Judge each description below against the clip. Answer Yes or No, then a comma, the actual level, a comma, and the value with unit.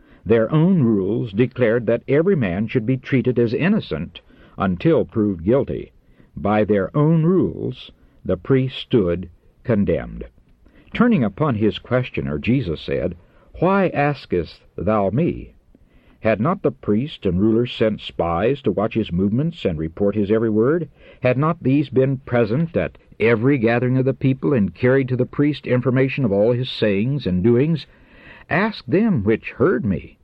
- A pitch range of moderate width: Yes, average, 4.8 semitones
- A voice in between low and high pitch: No, low, 125 Hz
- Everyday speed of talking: Yes, average, 155 wpm